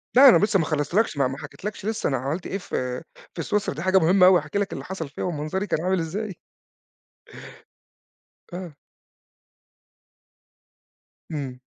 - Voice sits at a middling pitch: Yes, medium, 175 Hz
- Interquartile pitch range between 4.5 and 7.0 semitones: Yes, average, 5.0 semitones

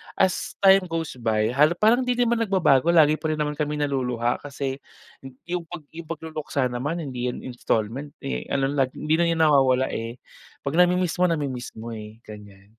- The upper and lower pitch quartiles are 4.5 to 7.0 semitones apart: Yes, average, 5.1 semitones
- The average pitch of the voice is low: No, medium, 145 Hz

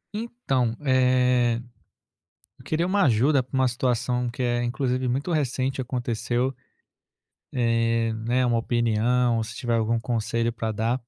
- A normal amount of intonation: No, narrow, 1.9 semitones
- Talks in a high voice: No, low, 125 Hz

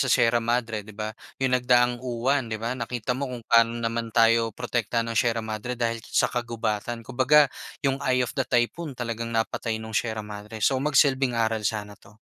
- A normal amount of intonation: No, narrow, 1.8 semitones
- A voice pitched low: Yes, low, 115 Hz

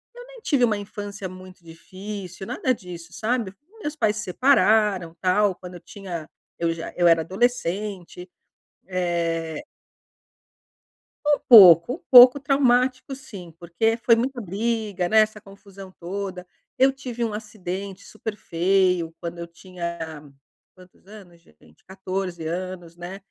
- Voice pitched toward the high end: Yes, high, 195 Hz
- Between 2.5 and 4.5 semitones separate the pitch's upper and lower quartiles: Yes, average, 4.2 semitones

